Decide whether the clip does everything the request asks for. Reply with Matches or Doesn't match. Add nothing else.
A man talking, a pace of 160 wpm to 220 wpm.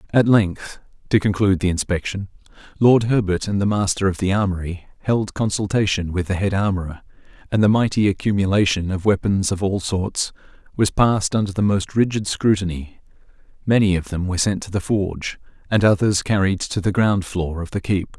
Matches